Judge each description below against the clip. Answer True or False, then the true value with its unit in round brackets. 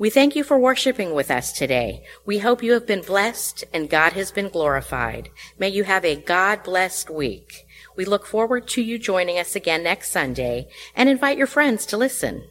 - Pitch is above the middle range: True (200 Hz)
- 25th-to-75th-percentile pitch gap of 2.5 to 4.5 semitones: False (5.2 semitones)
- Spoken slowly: False (195 wpm)